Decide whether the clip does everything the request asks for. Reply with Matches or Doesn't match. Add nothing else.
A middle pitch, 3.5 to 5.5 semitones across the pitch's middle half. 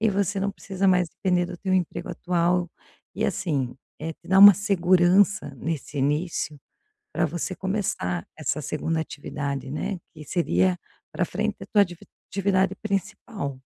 Matches